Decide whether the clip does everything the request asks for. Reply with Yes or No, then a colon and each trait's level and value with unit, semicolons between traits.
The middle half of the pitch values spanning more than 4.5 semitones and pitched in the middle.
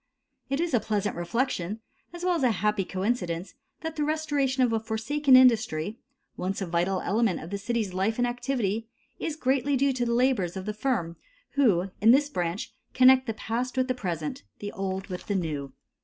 No: wide, 5.5 semitones; high, 225 Hz